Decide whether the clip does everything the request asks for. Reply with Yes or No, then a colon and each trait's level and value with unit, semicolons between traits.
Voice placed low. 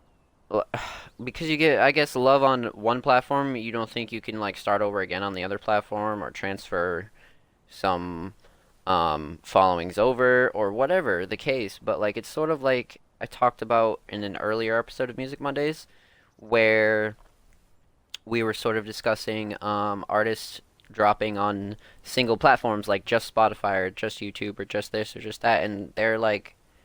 Yes: low, 110 Hz